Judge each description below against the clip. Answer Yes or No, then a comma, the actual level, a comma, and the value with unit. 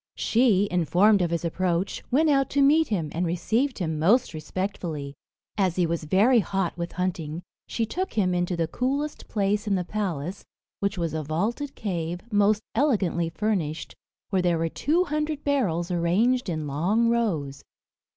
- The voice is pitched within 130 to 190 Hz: Yes, medium, 185 Hz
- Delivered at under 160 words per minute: No, average, 165 wpm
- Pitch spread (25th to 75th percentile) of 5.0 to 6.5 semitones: Yes, wide, 5.5 semitones